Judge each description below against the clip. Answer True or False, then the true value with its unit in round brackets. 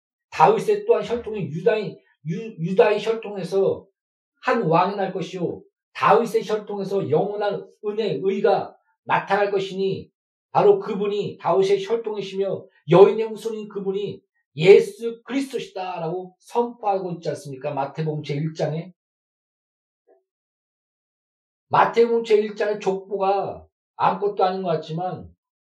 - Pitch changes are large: False (3.9 semitones)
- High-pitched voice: True (205 Hz)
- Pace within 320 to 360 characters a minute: False (270 characters per minute)